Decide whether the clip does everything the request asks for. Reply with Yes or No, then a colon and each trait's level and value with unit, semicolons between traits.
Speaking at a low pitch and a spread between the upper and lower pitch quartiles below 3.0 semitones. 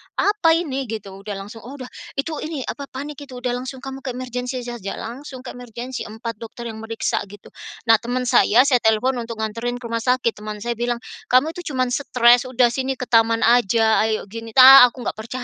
No: high, 245 Hz; narrow, 2.4 semitones